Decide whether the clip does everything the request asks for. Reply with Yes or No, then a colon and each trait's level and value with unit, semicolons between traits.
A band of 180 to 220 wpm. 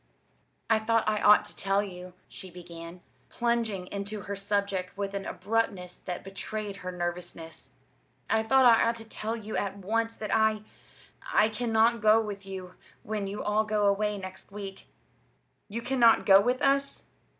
No: average, 165 wpm